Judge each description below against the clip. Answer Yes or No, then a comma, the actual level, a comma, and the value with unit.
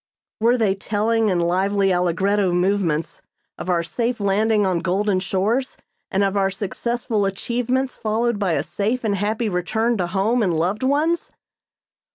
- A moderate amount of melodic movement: Yes, average, 3.5 semitones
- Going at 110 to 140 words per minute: No, average, 155 wpm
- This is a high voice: Yes, high, 200 Hz